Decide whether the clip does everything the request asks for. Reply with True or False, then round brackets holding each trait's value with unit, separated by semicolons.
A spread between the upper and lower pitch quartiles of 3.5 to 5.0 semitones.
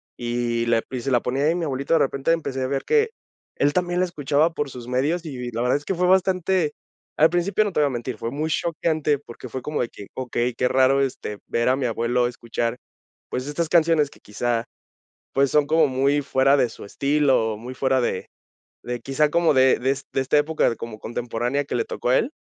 True (4.0 semitones)